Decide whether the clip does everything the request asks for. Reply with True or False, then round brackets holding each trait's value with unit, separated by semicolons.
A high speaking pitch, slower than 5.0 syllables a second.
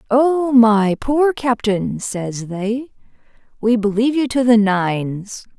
True (230 Hz; 3.5 syllables/s)